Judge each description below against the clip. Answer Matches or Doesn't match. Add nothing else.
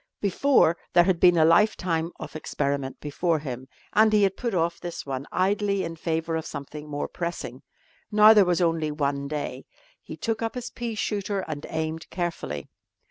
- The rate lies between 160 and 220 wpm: Matches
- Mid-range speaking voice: Matches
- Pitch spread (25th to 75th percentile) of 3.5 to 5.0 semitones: Matches